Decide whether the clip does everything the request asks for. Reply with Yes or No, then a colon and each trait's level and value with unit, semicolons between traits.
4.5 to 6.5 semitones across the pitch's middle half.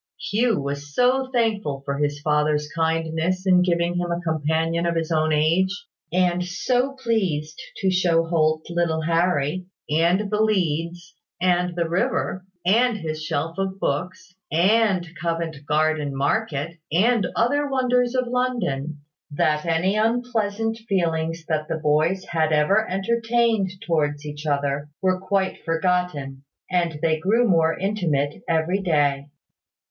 No: average, 3.9 semitones